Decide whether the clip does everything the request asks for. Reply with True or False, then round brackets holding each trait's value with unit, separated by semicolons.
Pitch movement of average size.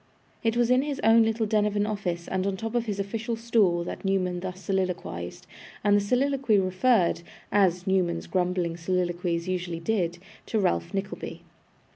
True (3.9 semitones)